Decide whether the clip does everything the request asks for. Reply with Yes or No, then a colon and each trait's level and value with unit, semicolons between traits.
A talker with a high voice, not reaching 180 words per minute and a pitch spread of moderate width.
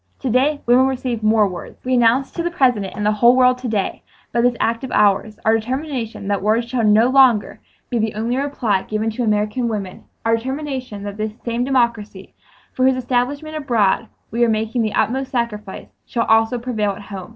No: high, 235 Hz; average, 195 wpm; average, 3.2 semitones